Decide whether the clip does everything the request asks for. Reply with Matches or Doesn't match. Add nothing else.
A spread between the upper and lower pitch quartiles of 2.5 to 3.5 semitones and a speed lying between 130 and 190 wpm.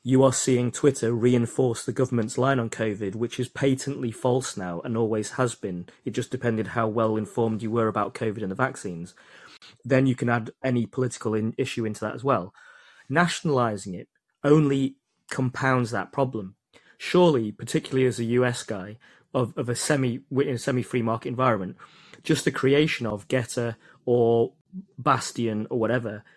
Matches